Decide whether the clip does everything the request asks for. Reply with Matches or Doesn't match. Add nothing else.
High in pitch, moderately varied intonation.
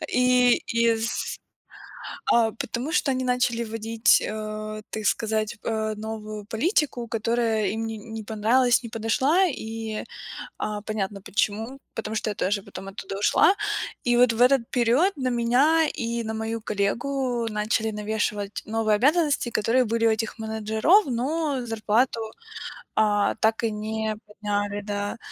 Doesn't match